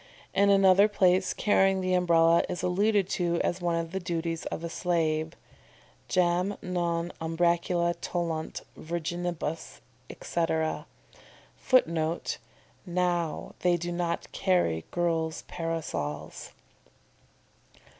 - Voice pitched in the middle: Yes, medium, 175 Hz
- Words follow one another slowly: Yes, slow, 105 wpm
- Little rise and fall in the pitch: Yes, narrow, 1.6 semitones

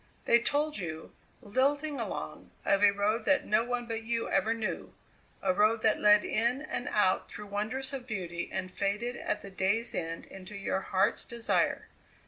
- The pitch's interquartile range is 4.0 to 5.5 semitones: No, average, 3.3 semitones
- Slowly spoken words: No, average, 175 wpm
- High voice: Yes, high, 215 Hz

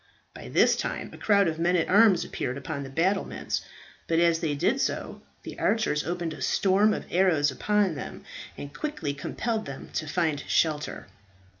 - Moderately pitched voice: Yes, medium, 170 Hz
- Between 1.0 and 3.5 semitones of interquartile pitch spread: No, average, 5.0 semitones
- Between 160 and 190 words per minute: Yes, average, 175 wpm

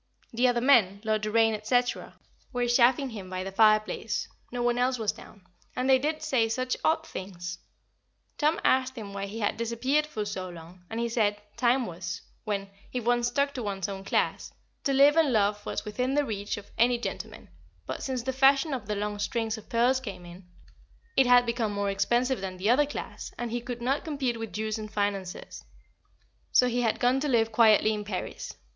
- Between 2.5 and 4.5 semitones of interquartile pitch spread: Yes, average, 3.7 semitones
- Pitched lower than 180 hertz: No, high, 230 Hz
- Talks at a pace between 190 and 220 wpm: Yes, average, 200 wpm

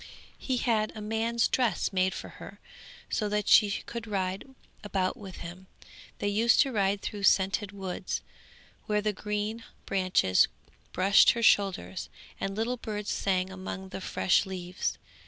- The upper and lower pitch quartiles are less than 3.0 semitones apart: Yes, narrow, 2.4 semitones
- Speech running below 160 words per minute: Yes, average, 150 wpm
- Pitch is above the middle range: Yes, high, 200 Hz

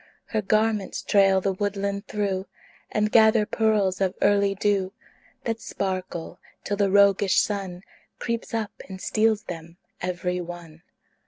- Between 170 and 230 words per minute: No, slow, 135 wpm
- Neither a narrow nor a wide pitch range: No, narrow, 2.2 semitones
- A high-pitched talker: Yes, high, 200 Hz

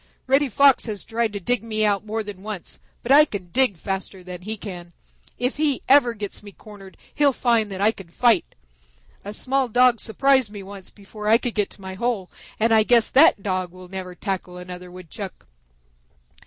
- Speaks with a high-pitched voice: Yes, high, 210 Hz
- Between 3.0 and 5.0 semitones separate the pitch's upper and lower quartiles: Yes, average, 4.1 semitones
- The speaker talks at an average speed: Yes, average, 195 wpm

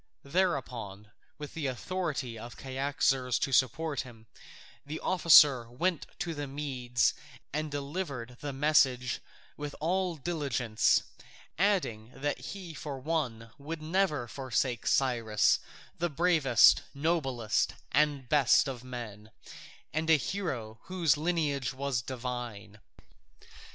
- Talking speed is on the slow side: Yes, slow, 115 wpm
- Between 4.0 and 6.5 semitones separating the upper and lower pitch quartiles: Yes, average, 4.4 semitones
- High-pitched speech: No, medium, 140 Hz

